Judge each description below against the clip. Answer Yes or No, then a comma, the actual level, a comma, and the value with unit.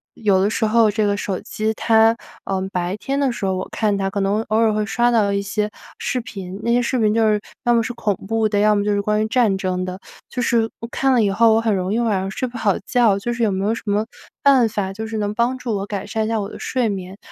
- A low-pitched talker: No, high, 215 Hz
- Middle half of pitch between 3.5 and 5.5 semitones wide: No, narrow, 2.4 semitones